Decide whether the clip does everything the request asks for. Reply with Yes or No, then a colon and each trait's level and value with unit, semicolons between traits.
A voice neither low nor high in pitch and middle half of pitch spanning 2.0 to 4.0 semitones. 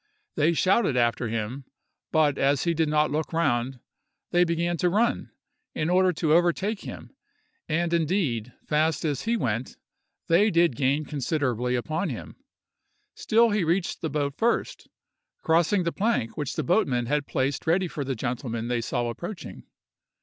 No: medium, 155 Hz; average, 5.1 semitones